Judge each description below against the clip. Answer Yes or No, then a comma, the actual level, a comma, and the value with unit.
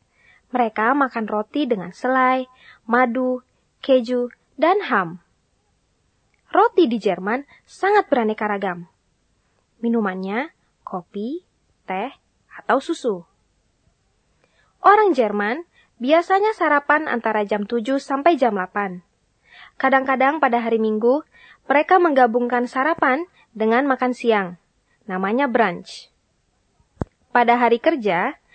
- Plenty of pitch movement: No, average, 4.5 semitones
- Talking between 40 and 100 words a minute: Yes, average, 95 wpm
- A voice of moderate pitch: No, very high, 250 Hz